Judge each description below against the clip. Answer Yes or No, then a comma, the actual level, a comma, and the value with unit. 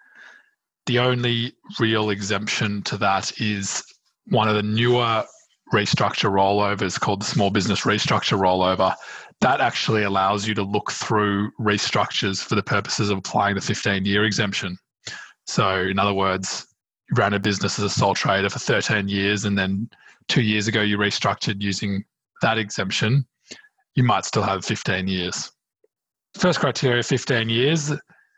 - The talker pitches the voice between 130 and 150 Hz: No, low, 105 Hz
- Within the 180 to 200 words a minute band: No, average, 150 wpm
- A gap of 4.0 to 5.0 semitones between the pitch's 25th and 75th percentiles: No, average, 3.1 semitones